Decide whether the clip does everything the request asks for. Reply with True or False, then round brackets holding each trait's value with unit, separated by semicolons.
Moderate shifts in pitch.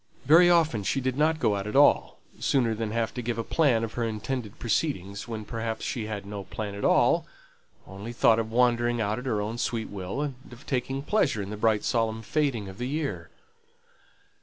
True (3.8 semitones)